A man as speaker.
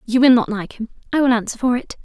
No: female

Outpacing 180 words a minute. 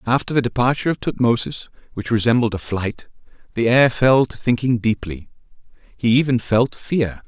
No: average, 155 wpm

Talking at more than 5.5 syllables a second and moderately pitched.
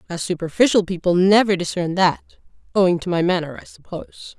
Yes: 5.8 syllables/s; medium, 180 Hz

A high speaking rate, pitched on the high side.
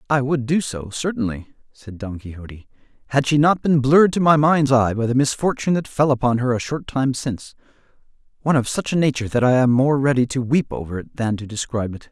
No: fast, 230 wpm; low, 130 Hz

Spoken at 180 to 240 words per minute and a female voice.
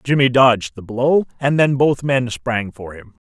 No: average, 200 wpm; male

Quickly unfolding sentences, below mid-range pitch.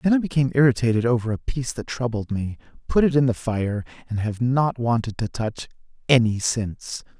No: average, 190 wpm; low, 120 Hz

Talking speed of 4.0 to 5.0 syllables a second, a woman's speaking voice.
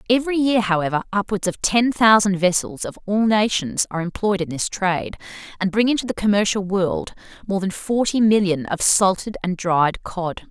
No: 5.2 syllables/s; female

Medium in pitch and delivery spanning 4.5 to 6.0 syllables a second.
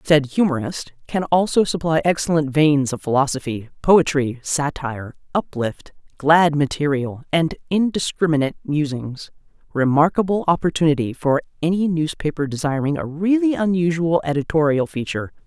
Yes: medium, 155 Hz; 5.1 syllables/s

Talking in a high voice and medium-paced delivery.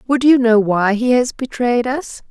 No: high, 240 Hz; fast, 210 wpm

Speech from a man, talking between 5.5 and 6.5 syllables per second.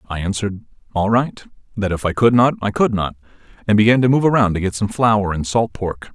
Yes: male; 5.8 syllables/s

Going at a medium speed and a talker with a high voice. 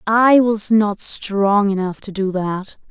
Yes: average, 165 wpm; high, 205 Hz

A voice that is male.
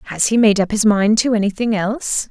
No: female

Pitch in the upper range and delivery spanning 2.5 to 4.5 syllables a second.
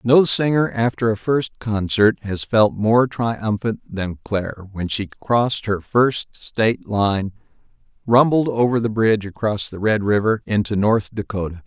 No: low, 110 Hz; 4.3 syllables/s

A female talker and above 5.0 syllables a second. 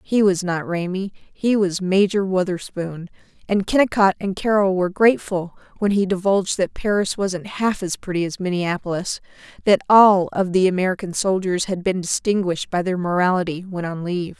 Yes: female; 5.2 syllables/s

